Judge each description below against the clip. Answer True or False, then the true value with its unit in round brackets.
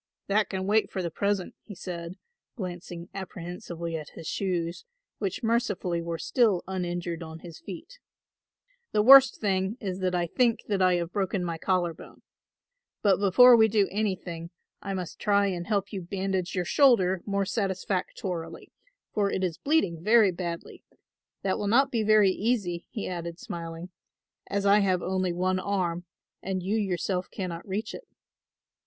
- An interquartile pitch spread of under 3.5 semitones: True (2.8 semitones)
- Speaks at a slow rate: False (160 wpm)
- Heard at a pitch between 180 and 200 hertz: True (190 Hz)